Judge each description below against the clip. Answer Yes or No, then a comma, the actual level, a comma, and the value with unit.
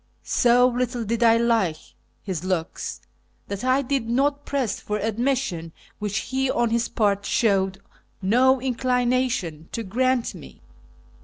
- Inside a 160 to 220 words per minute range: No, average, 140 wpm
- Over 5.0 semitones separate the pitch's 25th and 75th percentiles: No, average, 4.2 semitones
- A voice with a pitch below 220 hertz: No, high, 235 Hz